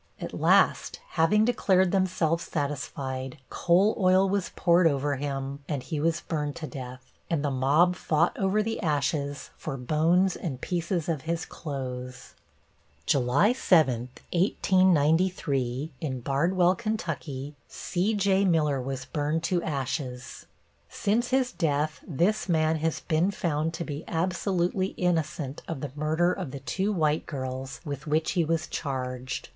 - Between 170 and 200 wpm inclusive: No, average, 140 wpm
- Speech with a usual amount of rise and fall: Yes, average, 4.5 semitones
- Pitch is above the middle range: No, medium, 160 Hz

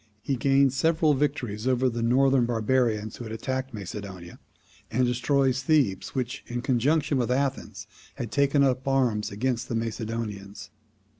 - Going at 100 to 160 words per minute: Yes, average, 145 wpm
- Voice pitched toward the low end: Yes, low, 125 Hz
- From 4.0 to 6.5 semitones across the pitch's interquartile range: No, average, 3.3 semitones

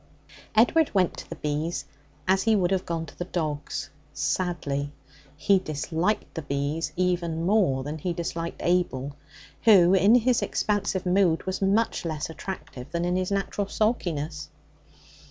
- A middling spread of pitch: Yes, average, 3.7 semitones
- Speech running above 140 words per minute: Yes, average, 150 wpm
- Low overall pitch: No, medium, 175 Hz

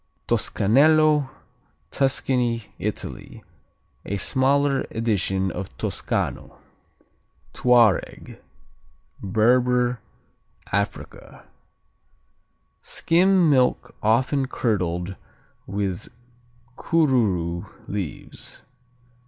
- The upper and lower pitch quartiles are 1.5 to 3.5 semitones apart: No, wide, 5.5 semitones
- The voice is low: Yes, low, 120 Hz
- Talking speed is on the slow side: Yes, slow, 55 wpm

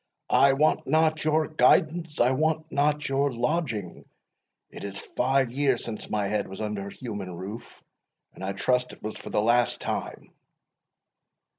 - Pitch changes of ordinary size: No, wide, 6.3 semitones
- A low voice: Yes, low, 125 Hz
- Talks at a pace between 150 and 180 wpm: Yes, average, 160 wpm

